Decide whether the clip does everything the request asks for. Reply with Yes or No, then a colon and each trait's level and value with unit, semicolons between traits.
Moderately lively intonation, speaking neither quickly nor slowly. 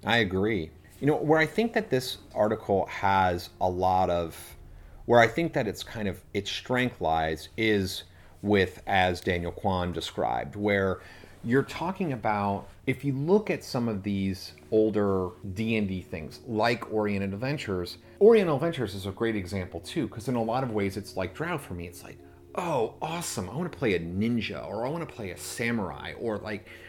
Yes: average, 4.2 semitones; average, 190 wpm